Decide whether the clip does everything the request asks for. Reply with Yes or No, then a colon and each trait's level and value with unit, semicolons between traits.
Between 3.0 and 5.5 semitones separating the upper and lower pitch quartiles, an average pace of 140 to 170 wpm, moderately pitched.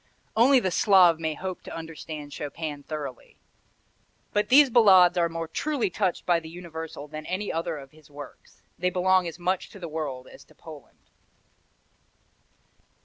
Yes: average, 3.3 semitones; average, 160 wpm; medium, 170 Hz